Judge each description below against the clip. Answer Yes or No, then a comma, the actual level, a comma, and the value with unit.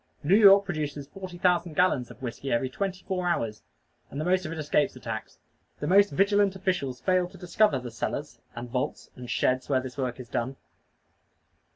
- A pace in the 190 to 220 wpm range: Yes, average, 195 wpm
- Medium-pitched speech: Yes, medium, 155 Hz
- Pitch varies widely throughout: Yes, wide, 6.5 semitones